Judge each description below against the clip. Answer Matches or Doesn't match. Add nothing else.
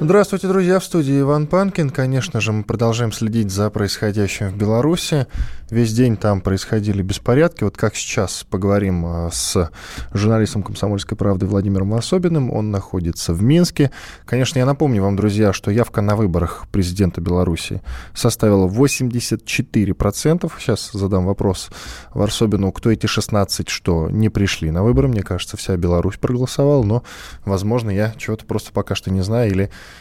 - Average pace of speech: Matches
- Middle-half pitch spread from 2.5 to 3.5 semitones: Doesn't match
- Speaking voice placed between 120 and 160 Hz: Doesn't match